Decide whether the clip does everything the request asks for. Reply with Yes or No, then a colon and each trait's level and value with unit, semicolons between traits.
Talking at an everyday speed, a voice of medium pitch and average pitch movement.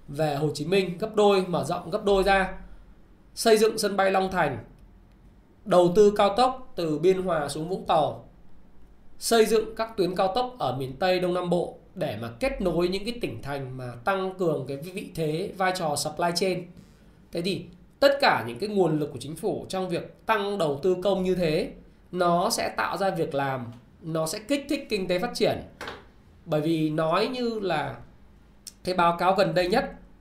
Yes: average, 200 wpm; medium, 180 Hz; average, 3.9 semitones